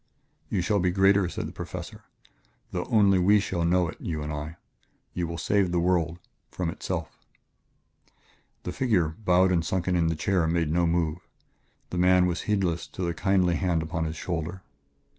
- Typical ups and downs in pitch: No, narrow, 2.2 semitones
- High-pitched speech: No, very low, 90 Hz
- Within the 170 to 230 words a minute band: Yes, average, 180 wpm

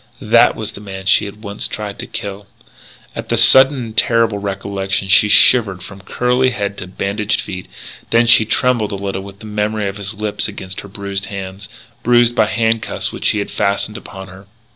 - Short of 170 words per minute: No, average, 195 wpm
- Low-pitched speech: Yes, low, 100 Hz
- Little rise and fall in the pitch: Yes, narrow, 2.0 semitones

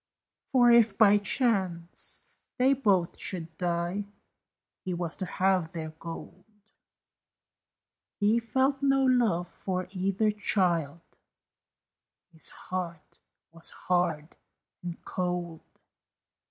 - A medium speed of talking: No, slow, 100 wpm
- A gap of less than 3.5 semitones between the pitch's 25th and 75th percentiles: No, average, 4.1 semitones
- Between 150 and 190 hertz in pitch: Yes, medium, 185 Hz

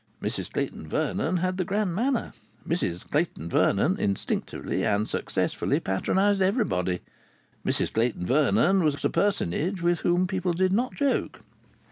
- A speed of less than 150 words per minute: Yes, slow, 135 wpm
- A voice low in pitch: No, medium, 175 Hz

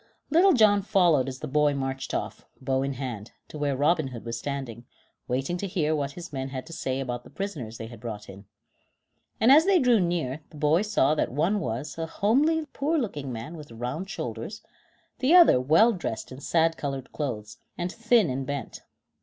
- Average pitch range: No, wide, 7.0 semitones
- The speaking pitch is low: No, medium, 145 Hz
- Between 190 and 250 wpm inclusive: Yes, average, 200 wpm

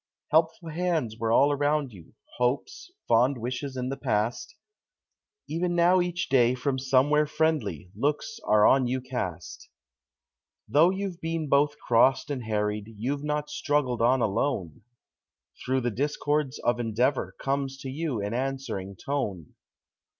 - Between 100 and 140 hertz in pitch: Yes, low, 135 Hz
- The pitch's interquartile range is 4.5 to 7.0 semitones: No, average, 4.1 semitones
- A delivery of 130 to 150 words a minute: Yes, average, 140 wpm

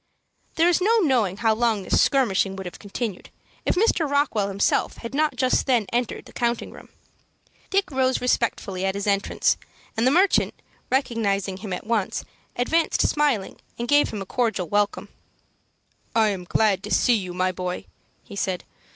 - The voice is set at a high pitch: Yes, high, 225 Hz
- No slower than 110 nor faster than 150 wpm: No, average, 170 wpm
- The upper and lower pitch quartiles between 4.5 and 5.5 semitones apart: Yes, average, 5.1 semitones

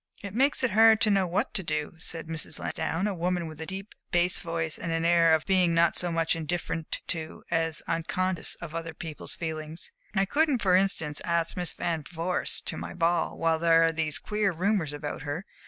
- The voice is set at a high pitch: No, medium, 170 Hz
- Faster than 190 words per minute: Yes, fast, 205 wpm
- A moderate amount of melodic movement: No, narrow, 2.3 semitones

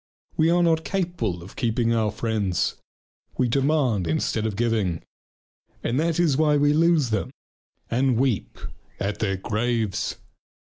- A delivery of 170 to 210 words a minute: No, average, 140 wpm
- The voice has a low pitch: Yes, low, 120 Hz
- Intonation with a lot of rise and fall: Yes, wide, 5.9 semitones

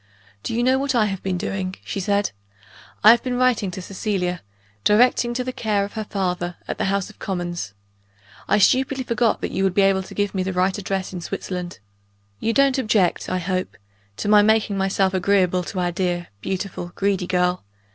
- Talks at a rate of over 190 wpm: Yes, average, 200 wpm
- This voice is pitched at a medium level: No, high, 195 Hz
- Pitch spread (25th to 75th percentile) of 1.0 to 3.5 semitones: Yes, average, 2.9 semitones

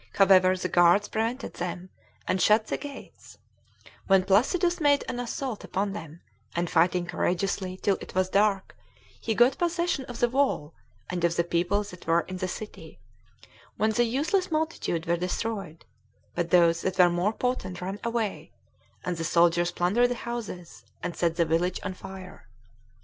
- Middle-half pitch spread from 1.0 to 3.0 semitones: No, average, 5.0 semitones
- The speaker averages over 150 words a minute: Yes, average, 165 wpm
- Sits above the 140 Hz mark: Yes, high, 190 Hz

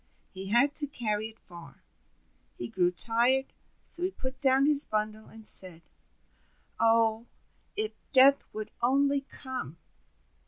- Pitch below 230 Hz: No, high, 235 Hz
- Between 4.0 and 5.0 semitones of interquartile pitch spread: Yes, average, 4.3 semitones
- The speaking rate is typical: No, slow, 130 wpm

